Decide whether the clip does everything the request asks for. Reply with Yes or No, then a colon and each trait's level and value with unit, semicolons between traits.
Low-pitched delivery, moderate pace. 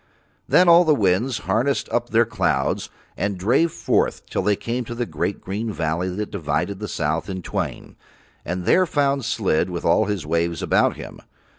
Yes: low, 105 Hz; average, 180 wpm